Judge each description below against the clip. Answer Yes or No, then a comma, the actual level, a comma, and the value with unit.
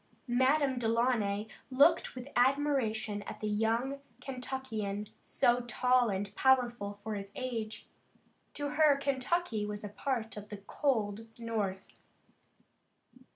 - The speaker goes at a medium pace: No, slow, 115 wpm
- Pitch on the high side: Yes, high, 235 Hz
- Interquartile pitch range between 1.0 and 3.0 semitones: No, average, 4.0 semitones